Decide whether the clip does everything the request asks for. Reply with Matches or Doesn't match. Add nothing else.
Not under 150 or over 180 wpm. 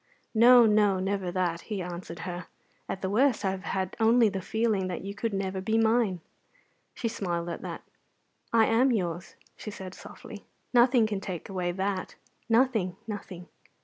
Matches